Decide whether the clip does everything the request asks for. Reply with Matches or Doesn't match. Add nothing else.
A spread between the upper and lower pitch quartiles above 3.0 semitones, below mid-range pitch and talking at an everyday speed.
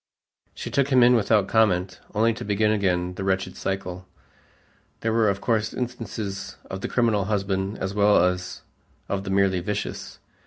Doesn't match